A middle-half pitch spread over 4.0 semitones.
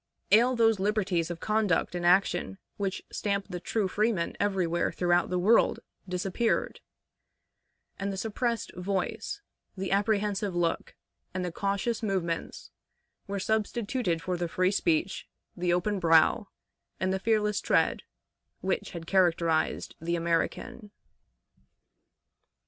No: average, 3.2 semitones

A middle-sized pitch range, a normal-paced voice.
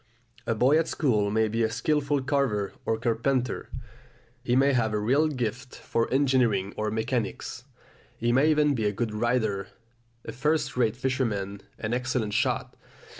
Yes: average, 3.7 semitones; average, 160 wpm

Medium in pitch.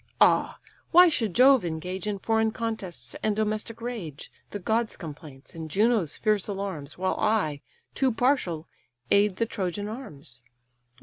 No: high, 205 Hz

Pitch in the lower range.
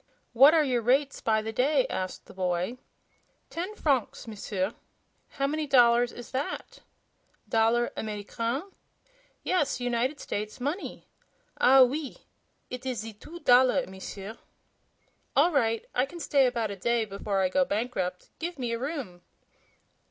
No: high, 245 Hz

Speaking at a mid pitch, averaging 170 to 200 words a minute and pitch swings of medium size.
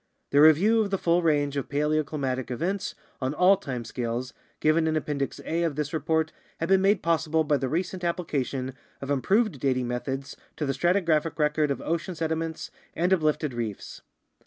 Yes: medium, 155 Hz; average, 175 wpm; average, 3.7 semitones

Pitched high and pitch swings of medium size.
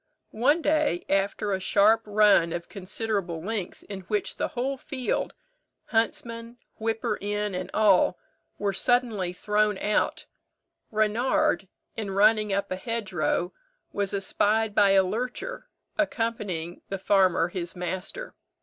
Yes: high, 210 Hz; average, 3.0 semitones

